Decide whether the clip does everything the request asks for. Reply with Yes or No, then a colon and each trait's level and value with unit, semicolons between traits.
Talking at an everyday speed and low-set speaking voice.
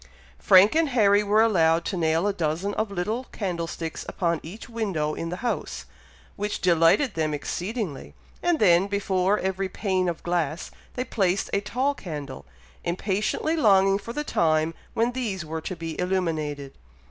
No: average, 160 wpm; high, 190 Hz